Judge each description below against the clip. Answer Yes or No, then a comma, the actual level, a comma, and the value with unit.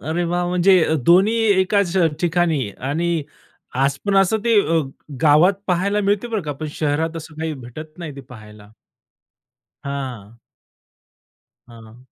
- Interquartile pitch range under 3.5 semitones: No, average, 4.7 semitones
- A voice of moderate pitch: Yes, medium, 160 Hz